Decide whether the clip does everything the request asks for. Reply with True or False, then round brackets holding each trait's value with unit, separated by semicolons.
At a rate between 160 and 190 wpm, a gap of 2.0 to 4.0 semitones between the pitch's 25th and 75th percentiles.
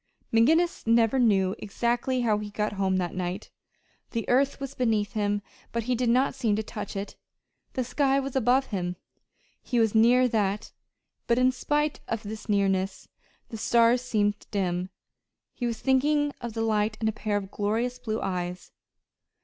True (170 wpm; 3.4 semitones)